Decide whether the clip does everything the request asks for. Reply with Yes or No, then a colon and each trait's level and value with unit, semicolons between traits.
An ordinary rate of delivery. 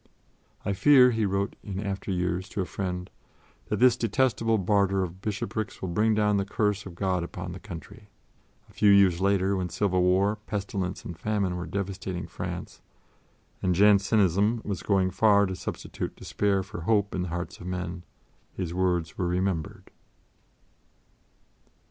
Yes: average, 160 wpm